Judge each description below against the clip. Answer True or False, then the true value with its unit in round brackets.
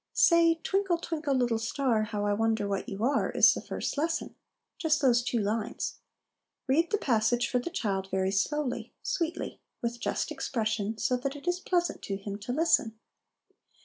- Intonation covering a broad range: True (6.9 semitones)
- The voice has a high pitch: True (245 Hz)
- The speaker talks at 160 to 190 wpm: True (180 wpm)